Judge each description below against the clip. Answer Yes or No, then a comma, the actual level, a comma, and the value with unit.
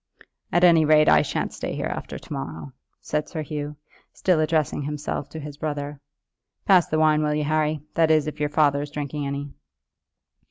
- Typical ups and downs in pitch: No, narrow, 1.3 semitones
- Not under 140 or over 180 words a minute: No, average, 190 wpm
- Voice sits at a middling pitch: Yes, medium, 150 Hz